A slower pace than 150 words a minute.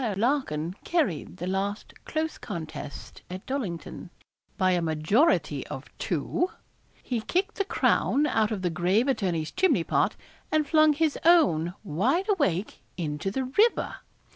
Yes: average, 140 wpm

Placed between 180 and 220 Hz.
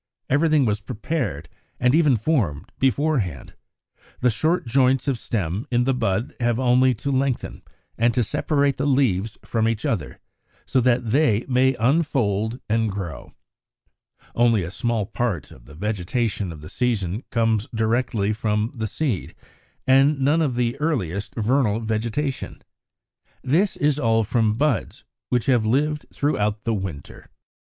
No: low, 120 Hz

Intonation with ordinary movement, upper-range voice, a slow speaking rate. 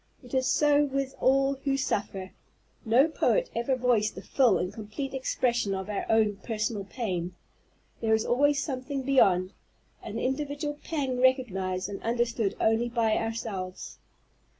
No: average, 4.6 semitones; high, 240 Hz; average, 145 wpm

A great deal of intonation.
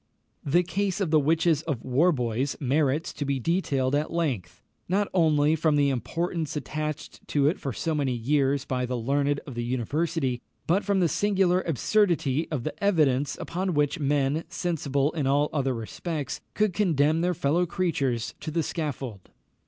No: average, 3.9 semitones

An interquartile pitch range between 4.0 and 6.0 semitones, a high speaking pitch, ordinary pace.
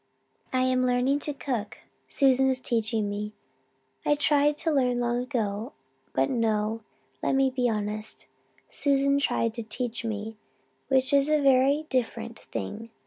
No: average, 3.5 semitones; very high, 250 Hz; average, 145 wpm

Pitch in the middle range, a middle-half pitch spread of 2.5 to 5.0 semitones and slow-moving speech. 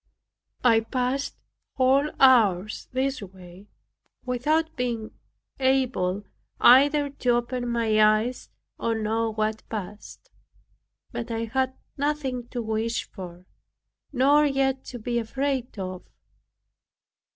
No: high, 240 Hz; average, 3.5 semitones; slow, 105 wpm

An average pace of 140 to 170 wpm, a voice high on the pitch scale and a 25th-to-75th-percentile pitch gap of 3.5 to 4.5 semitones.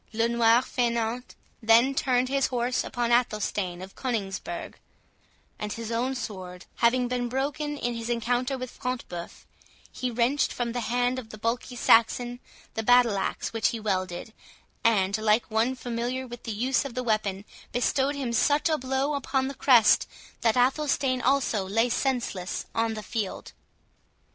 No: average, 165 wpm; high, 240 Hz; narrow, 2.5 semitones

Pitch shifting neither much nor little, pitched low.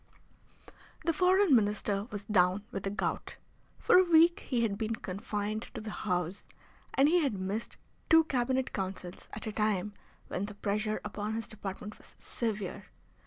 No: average, 3.8 semitones; high, 215 Hz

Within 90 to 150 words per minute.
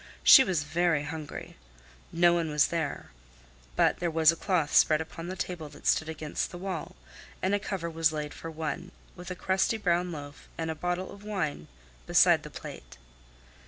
No: average, 185 wpm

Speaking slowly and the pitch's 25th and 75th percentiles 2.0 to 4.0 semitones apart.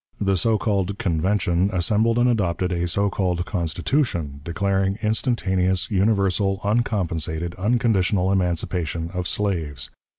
Yes: slow, 110 wpm; average, 3.0 semitones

